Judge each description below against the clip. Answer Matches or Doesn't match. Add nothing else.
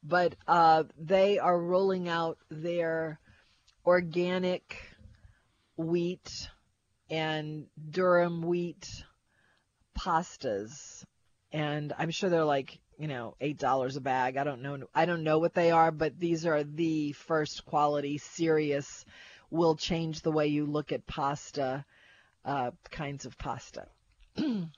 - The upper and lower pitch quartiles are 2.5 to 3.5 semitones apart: Matches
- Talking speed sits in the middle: Doesn't match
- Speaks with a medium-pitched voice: Matches